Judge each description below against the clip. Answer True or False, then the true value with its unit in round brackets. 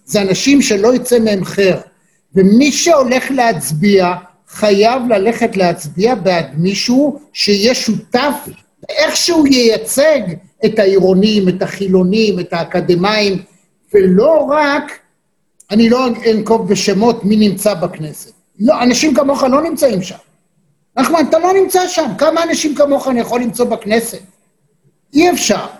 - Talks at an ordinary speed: True (125 wpm)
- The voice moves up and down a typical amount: False (6.0 semitones)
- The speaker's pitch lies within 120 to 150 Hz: False (215 Hz)